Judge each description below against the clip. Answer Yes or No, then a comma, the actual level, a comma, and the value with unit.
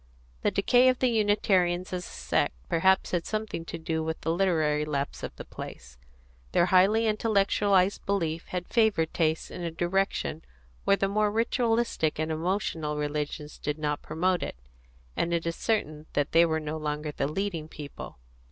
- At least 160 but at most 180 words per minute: Yes, average, 170 wpm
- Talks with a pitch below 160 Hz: No, medium, 170 Hz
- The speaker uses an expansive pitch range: No, average, 4.3 semitones